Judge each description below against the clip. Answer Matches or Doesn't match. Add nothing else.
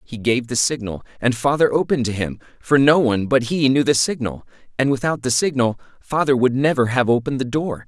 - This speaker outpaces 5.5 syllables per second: Matches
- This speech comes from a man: Matches